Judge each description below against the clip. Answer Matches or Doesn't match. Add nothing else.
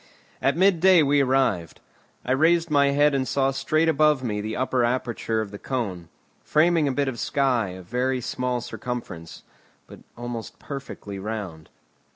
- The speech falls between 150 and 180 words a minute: Matches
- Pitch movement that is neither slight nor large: Matches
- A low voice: Matches